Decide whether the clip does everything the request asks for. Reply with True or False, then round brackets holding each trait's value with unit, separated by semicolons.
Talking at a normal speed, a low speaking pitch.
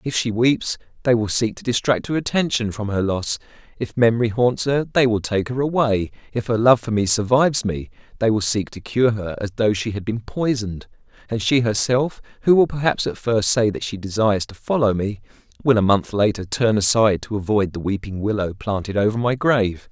False (215 wpm; 110 Hz)